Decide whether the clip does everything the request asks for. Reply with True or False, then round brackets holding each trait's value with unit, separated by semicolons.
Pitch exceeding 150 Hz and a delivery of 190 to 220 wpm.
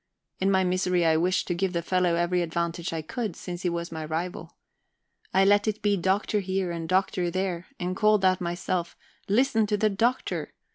True (185 Hz; 195 wpm)